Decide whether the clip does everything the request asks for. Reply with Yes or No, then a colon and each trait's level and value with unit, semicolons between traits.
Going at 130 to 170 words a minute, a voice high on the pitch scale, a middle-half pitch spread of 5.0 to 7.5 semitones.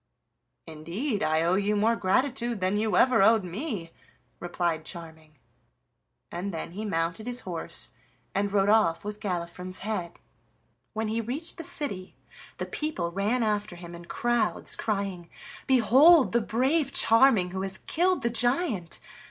Yes: average, 145 wpm; high, 205 Hz; average, 5.3 semitones